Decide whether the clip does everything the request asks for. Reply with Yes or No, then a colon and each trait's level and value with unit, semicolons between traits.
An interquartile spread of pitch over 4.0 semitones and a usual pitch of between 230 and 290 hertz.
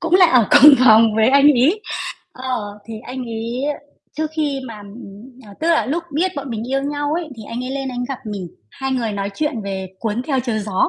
Yes: average, 4.6 semitones; very high, 250 Hz